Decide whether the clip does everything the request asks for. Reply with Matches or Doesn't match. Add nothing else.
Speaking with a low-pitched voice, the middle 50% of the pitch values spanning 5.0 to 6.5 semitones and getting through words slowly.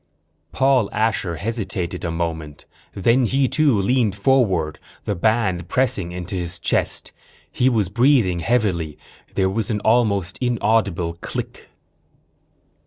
Matches